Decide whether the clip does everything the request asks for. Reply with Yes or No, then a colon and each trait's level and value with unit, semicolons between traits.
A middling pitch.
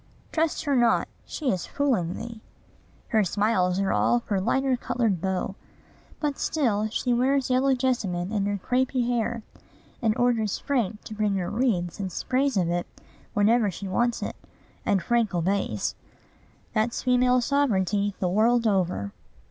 No: high, 220 Hz